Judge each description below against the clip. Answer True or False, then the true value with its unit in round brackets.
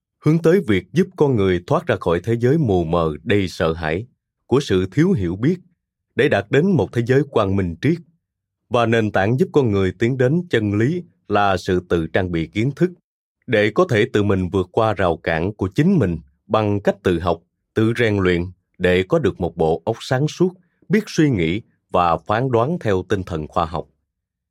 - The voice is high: False (105 Hz)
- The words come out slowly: False (210 wpm)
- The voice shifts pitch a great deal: True (7.0 semitones)